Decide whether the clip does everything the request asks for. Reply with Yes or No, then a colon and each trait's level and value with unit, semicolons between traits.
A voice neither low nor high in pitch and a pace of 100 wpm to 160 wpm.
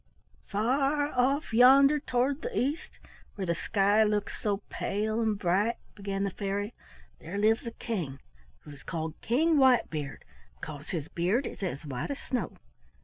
No: high, 210 Hz; average, 155 wpm